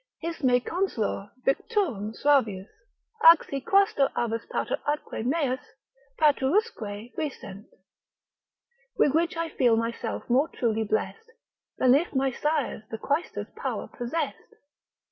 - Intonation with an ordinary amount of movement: No, wide, 6.2 semitones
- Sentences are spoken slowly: Yes, slow, 120 wpm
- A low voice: No, very high, 270 Hz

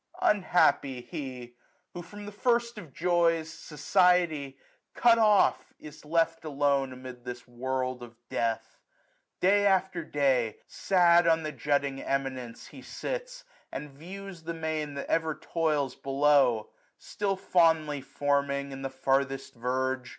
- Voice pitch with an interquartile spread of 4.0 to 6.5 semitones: Yes, average, 4.7 semitones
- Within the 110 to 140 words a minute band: Yes, slow, 135 wpm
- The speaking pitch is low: No, medium, 150 Hz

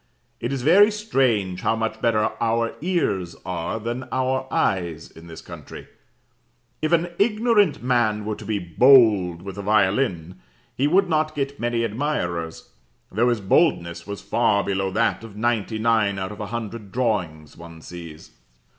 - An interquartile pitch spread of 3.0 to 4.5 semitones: No, wide, 5.6 semitones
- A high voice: No, low, 110 Hz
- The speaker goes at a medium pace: Yes, average, 160 wpm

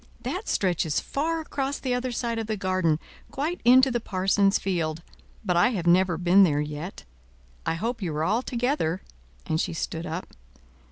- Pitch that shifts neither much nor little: No, wide, 6.5 semitones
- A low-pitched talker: No, high, 195 Hz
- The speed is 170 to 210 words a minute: Yes, average, 175 wpm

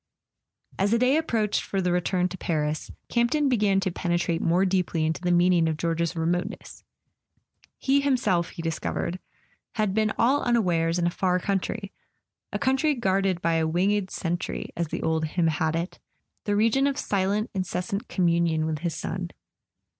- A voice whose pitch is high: No, medium, 180 Hz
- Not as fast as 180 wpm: Yes, average, 170 wpm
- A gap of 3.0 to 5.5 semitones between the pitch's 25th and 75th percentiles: Yes, average, 4.0 semitones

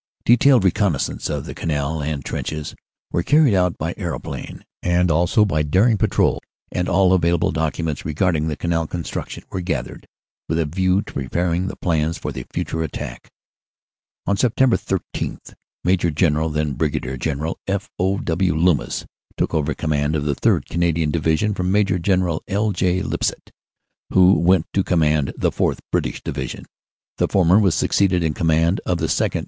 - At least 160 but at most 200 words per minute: Yes, average, 165 wpm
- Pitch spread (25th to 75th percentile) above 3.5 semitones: No, average, 3.2 semitones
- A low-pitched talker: Yes, very low, 85 Hz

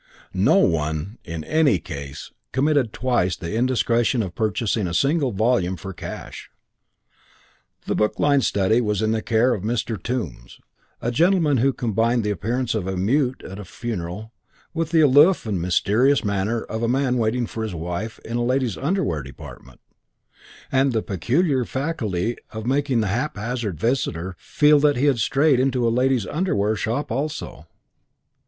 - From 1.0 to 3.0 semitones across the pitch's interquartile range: No, average, 4.9 semitones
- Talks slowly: No, average, 165 wpm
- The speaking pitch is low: Yes, low, 115 Hz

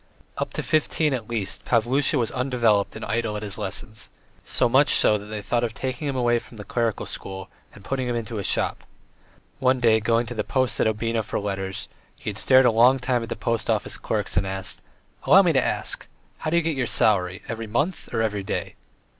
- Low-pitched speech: Yes, low, 115 Hz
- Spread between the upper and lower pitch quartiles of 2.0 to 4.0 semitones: Yes, average, 3.4 semitones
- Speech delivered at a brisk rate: Yes, fast, 220 wpm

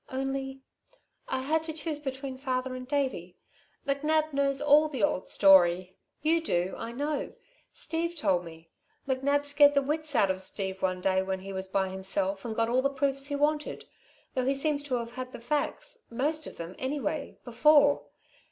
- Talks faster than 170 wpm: Yes, average, 180 wpm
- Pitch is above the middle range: Yes, very high, 265 Hz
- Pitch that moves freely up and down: Yes, wide, 6.8 semitones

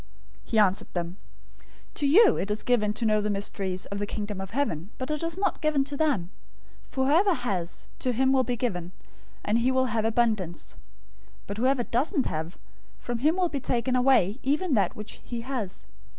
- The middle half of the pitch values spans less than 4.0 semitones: No, average, 5.1 semitones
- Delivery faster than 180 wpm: Yes, average, 200 wpm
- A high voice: Yes, high, 240 Hz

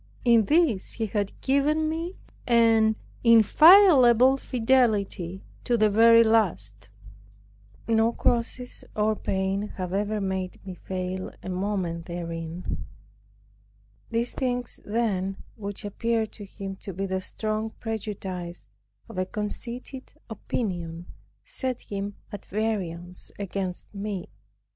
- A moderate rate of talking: No, slow, 115 wpm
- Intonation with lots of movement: No, average, 3.6 semitones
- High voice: Yes, high, 210 Hz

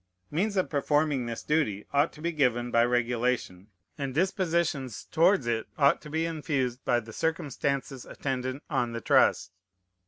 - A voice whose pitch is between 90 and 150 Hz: Yes, low, 135 Hz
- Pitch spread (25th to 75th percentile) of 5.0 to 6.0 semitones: No, average, 4.6 semitones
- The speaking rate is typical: Yes, average, 155 wpm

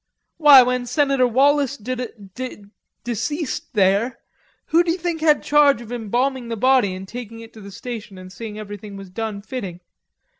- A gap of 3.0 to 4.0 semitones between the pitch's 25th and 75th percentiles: No, average, 4.6 semitones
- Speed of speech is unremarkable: Yes, average, 165 wpm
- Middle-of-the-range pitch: No, high, 240 Hz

